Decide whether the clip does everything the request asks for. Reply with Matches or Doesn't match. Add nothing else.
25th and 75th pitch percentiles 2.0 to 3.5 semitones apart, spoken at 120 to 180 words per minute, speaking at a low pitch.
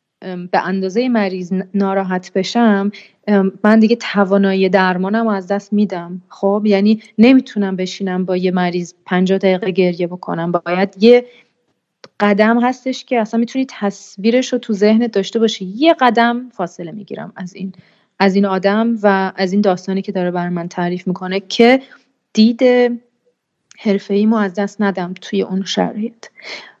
Doesn't match